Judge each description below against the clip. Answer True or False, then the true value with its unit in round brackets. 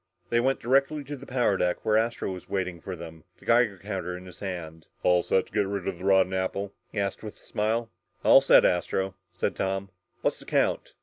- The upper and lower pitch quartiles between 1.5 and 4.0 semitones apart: True (3.4 semitones)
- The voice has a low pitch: True (95 Hz)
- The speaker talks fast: True (225 wpm)